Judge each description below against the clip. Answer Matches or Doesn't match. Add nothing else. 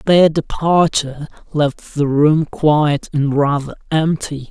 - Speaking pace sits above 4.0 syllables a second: Doesn't match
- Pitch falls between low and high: Matches